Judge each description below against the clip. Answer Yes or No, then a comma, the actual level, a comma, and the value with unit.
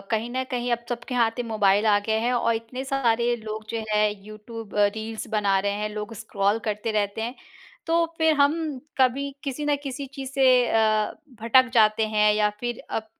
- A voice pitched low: No, high, 225 Hz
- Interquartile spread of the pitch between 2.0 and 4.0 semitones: Yes, average, 2.9 semitones